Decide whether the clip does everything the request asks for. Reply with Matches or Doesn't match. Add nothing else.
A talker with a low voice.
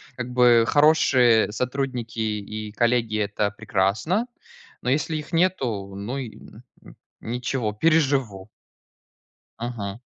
Matches